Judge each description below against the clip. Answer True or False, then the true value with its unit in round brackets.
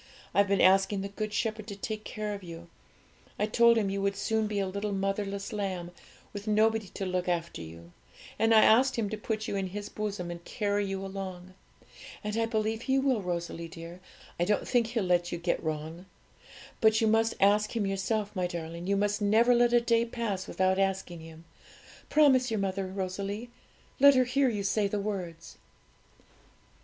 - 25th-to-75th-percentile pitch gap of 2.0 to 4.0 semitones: True (2.8 semitones)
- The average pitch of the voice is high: True (200 Hz)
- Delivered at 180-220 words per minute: True (190 wpm)